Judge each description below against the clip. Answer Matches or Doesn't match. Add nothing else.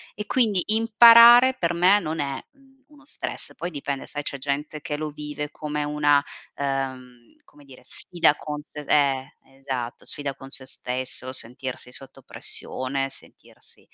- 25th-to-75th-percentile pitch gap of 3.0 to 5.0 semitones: Matches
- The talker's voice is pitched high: Doesn't match